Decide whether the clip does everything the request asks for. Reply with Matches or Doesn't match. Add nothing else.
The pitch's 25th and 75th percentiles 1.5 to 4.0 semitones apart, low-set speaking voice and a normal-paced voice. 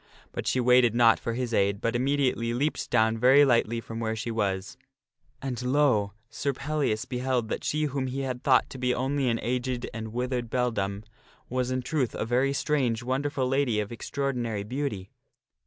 Matches